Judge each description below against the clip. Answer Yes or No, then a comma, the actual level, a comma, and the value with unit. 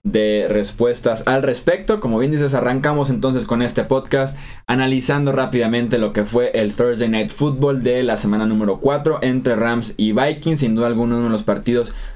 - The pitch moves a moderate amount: Yes, average, 3.0 semitones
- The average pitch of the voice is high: No, low, 125 Hz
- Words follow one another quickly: No, average, 180 wpm